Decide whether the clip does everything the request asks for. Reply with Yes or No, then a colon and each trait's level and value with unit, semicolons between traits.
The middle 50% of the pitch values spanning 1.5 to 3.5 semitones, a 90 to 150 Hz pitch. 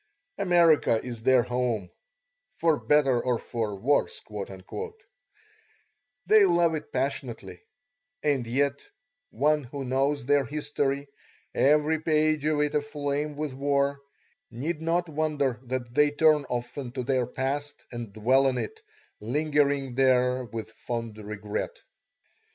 Yes: average, 3.2 semitones; medium, 140 Hz